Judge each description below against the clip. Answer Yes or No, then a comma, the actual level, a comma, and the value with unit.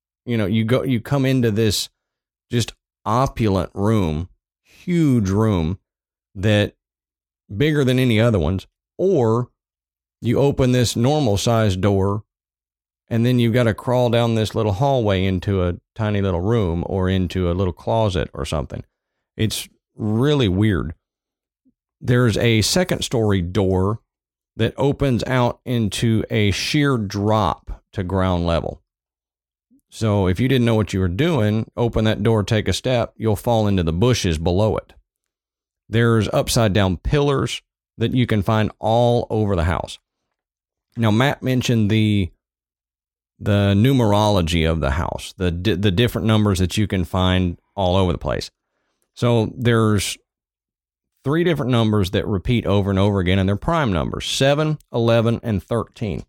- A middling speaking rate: Yes, average, 150 wpm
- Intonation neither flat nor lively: Yes, average, 4.4 semitones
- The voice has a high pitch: No, low, 105 Hz